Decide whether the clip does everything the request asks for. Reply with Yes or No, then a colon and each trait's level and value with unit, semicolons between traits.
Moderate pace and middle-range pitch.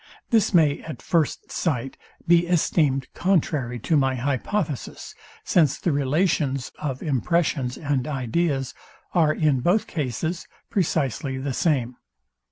No: slow, 120 wpm; medium, 145 Hz